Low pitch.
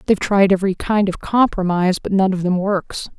No: high, 190 Hz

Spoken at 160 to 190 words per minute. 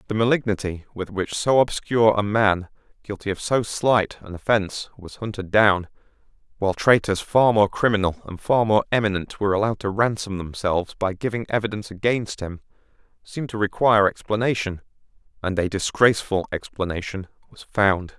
No: average, 150 wpm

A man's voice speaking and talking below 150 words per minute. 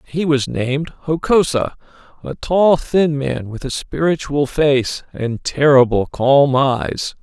Yes: male; slow, 135 wpm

